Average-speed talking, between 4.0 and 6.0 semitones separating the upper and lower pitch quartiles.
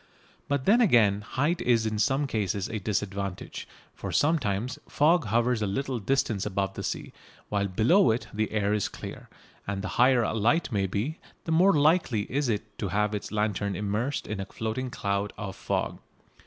Yes: average, 180 wpm; average, 4.7 semitones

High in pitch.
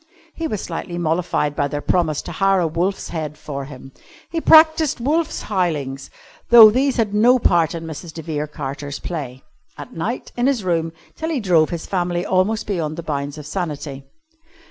No: medium, 170 Hz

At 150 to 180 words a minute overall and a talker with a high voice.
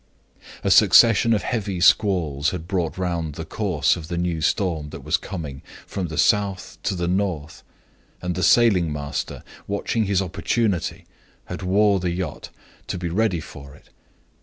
No: average, 160 wpm; very low, 90 Hz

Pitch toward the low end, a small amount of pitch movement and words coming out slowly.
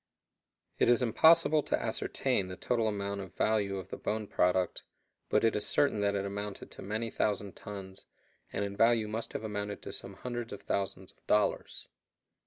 No: low, 105 Hz; narrow, 2.2 semitones; average, 185 wpm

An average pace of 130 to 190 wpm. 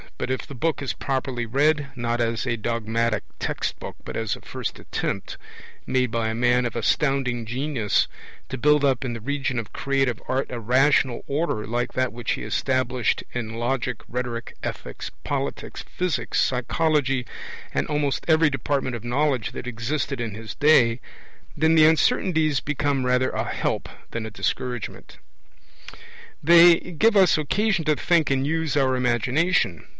Yes: average, 160 wpm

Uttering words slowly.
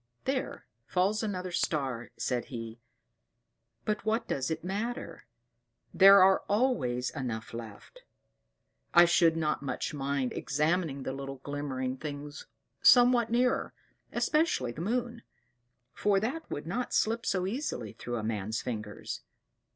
Yes: slow, 130 wpm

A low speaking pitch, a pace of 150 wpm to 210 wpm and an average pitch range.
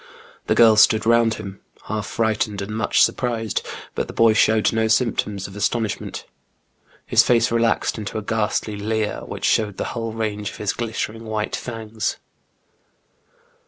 No: low, 110 Hz; average, 160 wpm; narrow, 1.2 semitones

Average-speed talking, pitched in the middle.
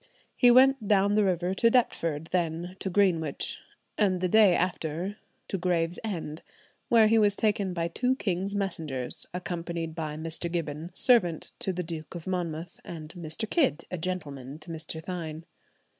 Yes: average, 155 wpm; medium, 175 Hz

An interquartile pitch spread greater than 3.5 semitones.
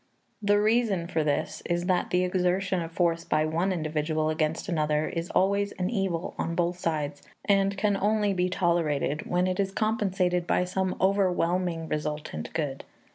No: average, 3.2 semitones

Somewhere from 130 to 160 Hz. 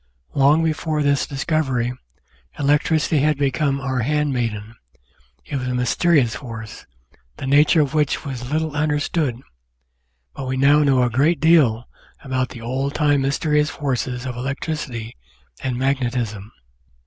Yes: low, 135 Hz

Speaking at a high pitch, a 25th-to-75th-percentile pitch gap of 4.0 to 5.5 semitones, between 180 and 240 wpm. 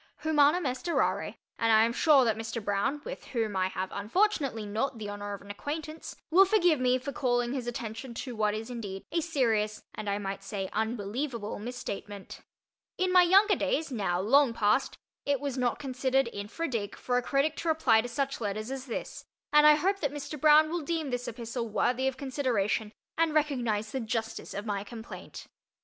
Yes: high, 245 Hz; average, 5.2 semitones; average, 195 wpm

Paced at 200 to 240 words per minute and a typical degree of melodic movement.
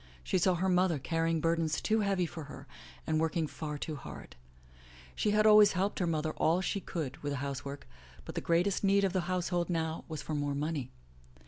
Yes: fast, 205 wpm; average, 3.7 semitones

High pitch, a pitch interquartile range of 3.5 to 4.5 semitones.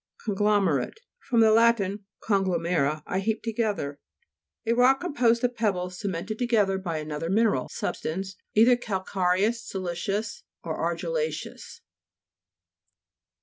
Yes: high, 205 Hz; average, 4.1 semitones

